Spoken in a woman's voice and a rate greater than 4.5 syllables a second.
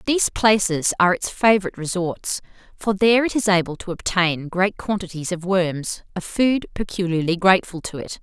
Yes: female; 5.3 syllables/s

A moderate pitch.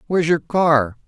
Yes: medium, 155 Hz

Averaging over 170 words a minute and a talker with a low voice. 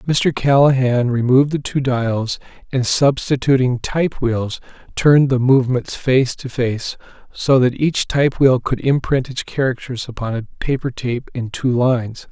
No: average, 155 wpm; low, 130 Hz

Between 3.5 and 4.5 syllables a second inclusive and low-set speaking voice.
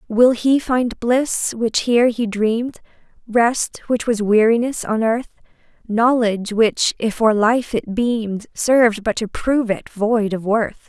No: 4.1 syllables/s; high, 230 Hz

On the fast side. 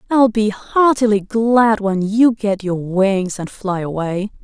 No: average, 160 wpm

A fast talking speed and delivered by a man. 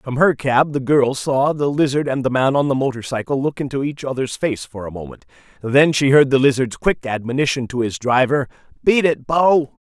Yes: fast, 215 wpm; male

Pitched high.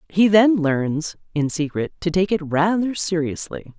No: medium, 170 Hz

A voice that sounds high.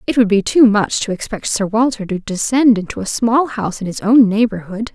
Yes: high, 215 Hz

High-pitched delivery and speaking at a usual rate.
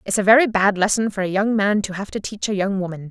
No: high, 200 Hz; fast, 310 wpm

